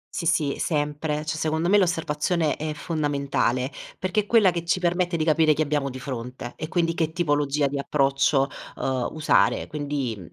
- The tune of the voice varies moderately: Yes, average, 3.1 semitones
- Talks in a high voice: No, medium, 150 Hz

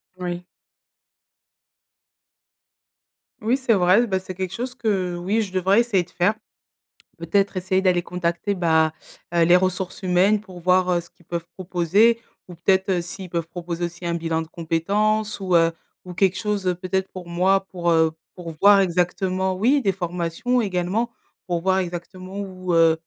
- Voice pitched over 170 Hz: Yes, medium, 185 Hz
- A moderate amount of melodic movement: No, narrow, 2.1 semitones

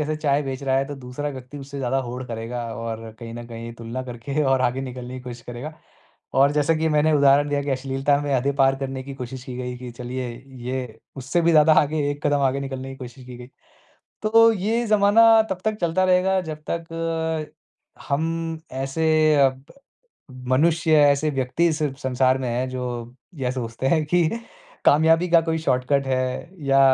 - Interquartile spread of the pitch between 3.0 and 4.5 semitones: Yes, average, 3.6 semitones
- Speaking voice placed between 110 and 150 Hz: Yes, low, 135 Hz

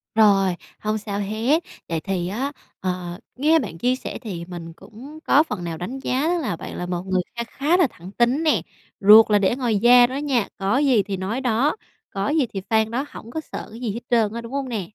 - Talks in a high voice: Yes, high, 220 Hz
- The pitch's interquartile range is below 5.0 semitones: No, average, 5.3 semitones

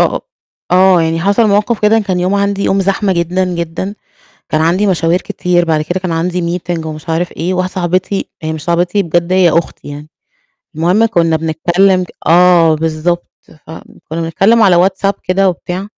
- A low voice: No, medium, 175 Hz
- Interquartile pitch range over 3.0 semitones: No, narrow, 2.6 semitones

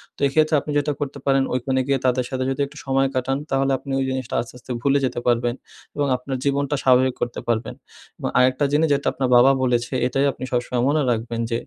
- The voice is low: Yes, low, 130 Hz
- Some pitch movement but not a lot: No, narrow, 2.0 semitones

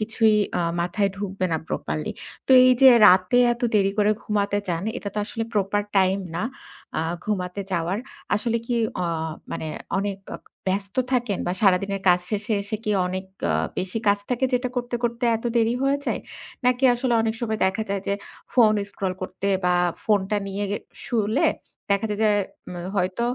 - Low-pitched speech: No, high, 205 Hz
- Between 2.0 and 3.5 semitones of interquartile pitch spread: Yes, average, 3.1 semitones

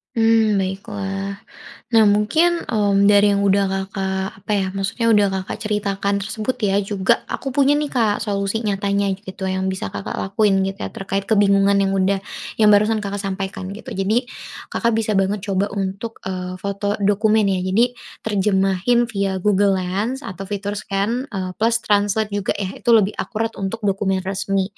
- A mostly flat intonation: Yes, narrow, 1.8 semitones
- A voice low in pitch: No, high, 200 Hz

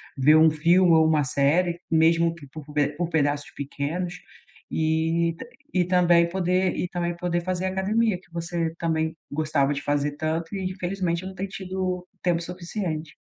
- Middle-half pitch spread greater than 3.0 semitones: No, narrow, 2.4 semitones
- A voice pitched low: No, medium, 170 Hz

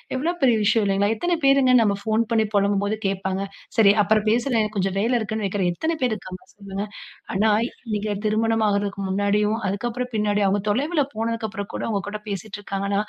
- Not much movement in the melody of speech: Yes, narrow, 2.2 semitones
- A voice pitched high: Yes, high, 210 Hz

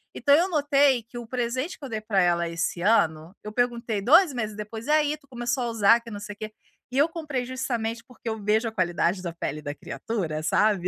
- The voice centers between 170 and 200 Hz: No, high, 230 Hz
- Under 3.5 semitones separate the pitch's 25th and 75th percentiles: No, average, 4.3 semitones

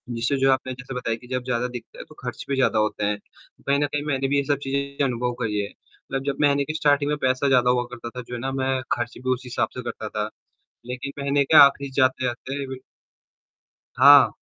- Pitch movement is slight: Yes, narrow, 2.2 semitones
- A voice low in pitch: Yes, low, 130 Hz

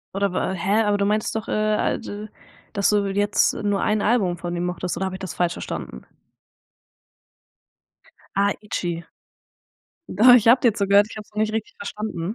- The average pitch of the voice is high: Yes, high, 200 Hz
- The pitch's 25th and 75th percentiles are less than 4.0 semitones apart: Yes, narrow, 2.5 semitones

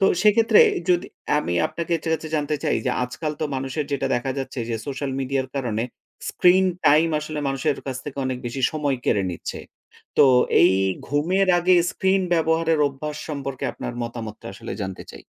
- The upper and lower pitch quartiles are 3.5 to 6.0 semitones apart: Yes, average, 3.8 semitones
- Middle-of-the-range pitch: Yes, medium, 145 Hz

